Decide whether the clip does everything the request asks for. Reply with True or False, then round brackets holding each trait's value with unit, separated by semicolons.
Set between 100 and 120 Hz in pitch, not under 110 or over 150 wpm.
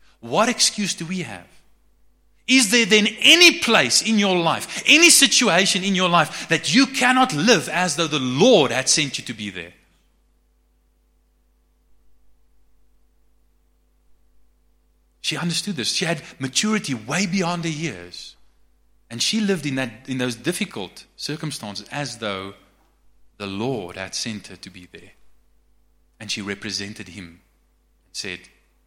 True (115 Hz; 140 wpm)